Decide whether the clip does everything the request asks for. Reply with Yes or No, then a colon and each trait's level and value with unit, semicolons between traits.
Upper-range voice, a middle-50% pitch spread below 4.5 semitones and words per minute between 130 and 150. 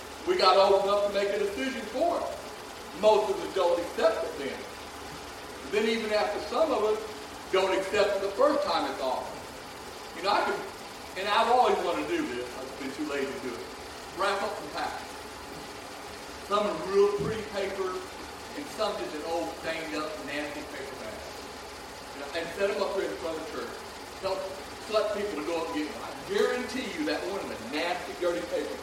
No: high, 200 Hz; narrow, 2.5 semitones; fast, 205 wpm